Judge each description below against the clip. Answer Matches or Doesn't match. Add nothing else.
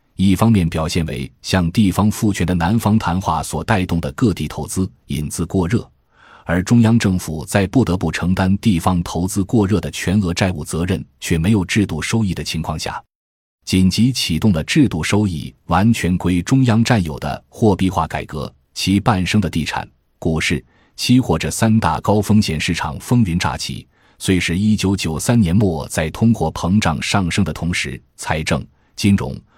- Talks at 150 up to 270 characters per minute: Matches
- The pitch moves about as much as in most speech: Matches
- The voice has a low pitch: Matches